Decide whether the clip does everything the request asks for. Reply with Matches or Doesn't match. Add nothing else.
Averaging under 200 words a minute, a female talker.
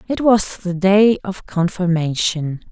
Matches